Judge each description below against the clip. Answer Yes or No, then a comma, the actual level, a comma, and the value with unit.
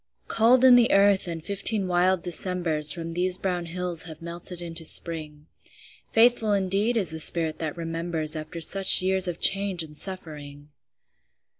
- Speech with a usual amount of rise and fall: Yes, average, 3.0 semitones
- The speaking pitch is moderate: Yes, medium, 175 Hz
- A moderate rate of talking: Yes, average, 155 wpm